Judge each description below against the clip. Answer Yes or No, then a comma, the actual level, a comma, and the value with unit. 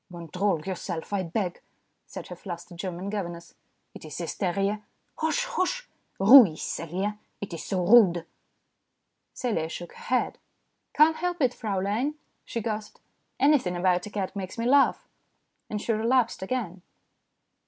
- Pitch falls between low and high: No, high, 200 Hz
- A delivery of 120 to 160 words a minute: Yes, average, 150 wpm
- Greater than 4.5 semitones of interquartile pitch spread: Yes, average, 5.2 semitones